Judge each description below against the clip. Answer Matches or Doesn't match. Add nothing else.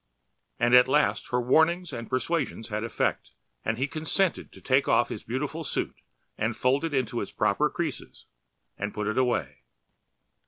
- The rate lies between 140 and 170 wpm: Matches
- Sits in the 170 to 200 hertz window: Doesn't match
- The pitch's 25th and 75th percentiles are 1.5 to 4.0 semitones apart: Doesn't match